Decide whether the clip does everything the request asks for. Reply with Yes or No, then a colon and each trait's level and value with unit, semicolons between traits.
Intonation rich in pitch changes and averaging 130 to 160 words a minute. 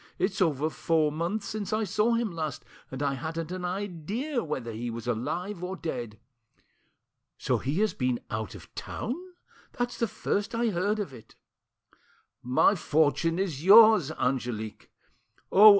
Yes: wide, 7.5 semitones; average, 150 wpm